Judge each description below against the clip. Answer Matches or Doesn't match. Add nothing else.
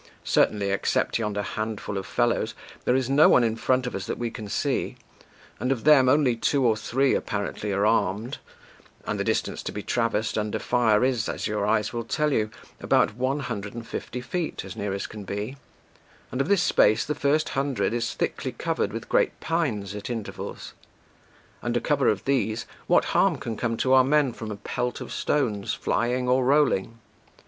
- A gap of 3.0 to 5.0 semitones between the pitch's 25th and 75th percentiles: Matches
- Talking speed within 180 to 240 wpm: Matches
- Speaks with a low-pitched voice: Matches